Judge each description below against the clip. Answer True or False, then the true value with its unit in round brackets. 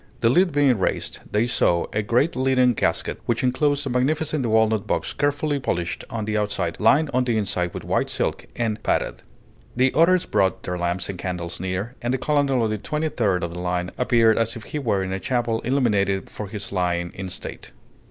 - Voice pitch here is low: True (115 Hz)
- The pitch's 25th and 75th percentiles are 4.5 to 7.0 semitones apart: True (5.5 semitones)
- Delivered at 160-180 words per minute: False (205 wpm)